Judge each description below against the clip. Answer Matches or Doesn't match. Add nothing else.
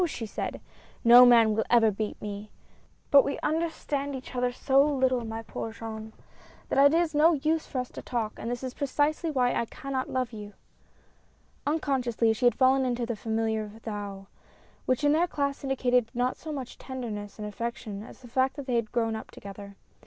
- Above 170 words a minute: Matches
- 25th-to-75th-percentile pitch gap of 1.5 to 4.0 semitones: Matches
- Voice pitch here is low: Doesn't match